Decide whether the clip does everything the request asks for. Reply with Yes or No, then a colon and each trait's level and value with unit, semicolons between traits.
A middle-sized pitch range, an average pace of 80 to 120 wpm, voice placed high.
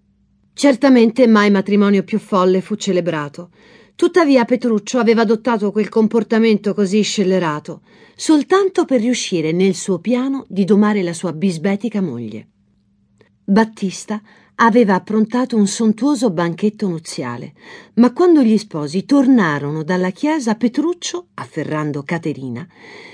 Yes: average, 4.8 semitones; slow, 115 wpm; high, 210 Hz